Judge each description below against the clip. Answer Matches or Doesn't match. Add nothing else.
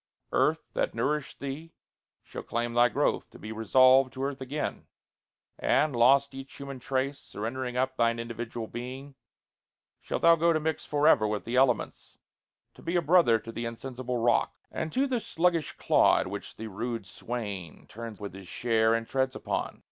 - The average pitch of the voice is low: Matches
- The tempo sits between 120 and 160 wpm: Doesn't match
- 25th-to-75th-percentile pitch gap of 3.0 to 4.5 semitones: Matches